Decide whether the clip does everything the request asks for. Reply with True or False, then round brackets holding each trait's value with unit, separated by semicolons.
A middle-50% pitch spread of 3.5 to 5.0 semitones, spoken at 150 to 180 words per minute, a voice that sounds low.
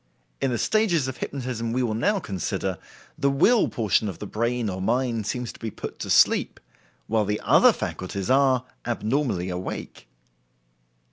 True (3.9 semitones; 160 wpm; 120 Hz)